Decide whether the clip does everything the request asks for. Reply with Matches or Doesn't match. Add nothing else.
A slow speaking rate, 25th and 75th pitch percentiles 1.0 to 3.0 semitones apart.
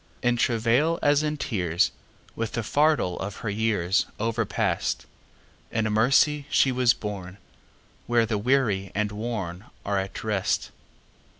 Doesn't match